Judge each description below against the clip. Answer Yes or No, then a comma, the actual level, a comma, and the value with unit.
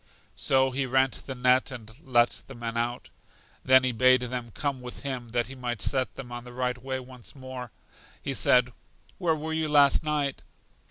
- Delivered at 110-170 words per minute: No, average, 195 wpm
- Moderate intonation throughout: No, narrow, 1.6 semitones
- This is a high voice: No, low, 130 Hz